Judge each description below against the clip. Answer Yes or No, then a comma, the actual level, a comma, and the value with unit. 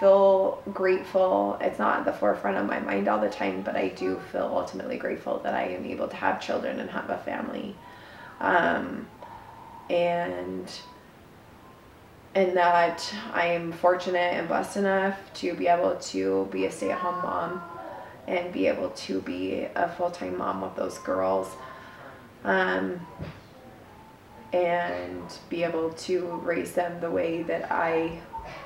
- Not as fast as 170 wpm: Yes, average, 145 wpm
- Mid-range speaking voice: Yes, medium, 175 Hz